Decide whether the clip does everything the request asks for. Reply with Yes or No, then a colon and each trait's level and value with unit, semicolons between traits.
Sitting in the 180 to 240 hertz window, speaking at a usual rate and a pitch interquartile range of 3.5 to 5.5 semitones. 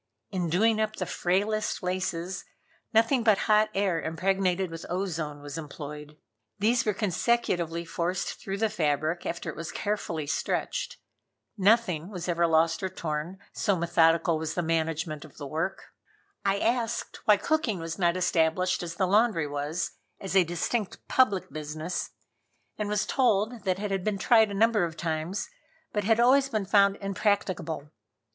Yes: medium, 185 Hz; average, 160 wpm; average, 4.2 semitones